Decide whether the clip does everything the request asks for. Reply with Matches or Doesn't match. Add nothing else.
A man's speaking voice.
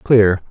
Matches